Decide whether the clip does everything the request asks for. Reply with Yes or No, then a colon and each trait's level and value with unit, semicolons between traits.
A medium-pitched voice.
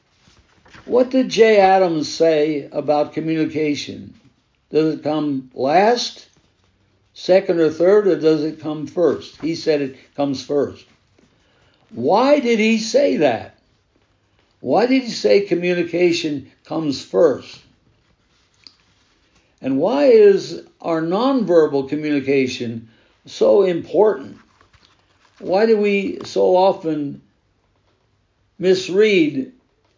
Yes: medium, 155 Hz